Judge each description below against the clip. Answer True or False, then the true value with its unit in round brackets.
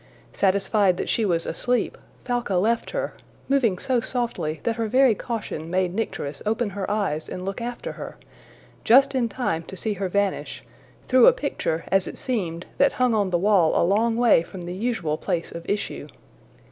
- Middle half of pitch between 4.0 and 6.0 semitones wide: True (4.9 semitones)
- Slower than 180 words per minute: False (185 wpm)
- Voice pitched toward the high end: True (205 Hz)